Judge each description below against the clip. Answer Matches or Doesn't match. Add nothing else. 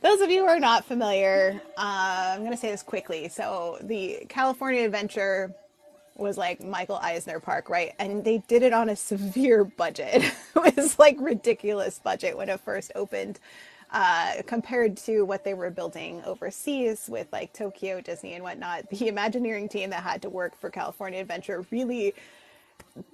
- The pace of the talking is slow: Doesn't match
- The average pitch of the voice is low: Doesn't match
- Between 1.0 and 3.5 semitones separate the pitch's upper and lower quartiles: Doesn't match